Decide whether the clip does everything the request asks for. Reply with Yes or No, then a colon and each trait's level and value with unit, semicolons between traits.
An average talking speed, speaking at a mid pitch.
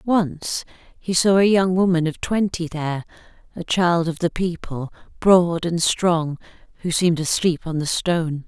Yes: average, 165 wpm; medium, 170 Hz